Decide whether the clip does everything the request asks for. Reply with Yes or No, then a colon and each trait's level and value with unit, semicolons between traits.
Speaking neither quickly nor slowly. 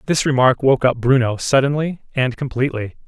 Yes: average, 155 wpm